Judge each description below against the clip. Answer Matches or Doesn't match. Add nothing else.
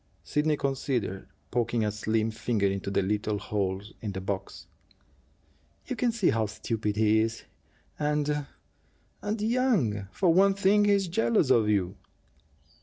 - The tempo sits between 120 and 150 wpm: Matches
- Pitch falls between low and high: Doesn't match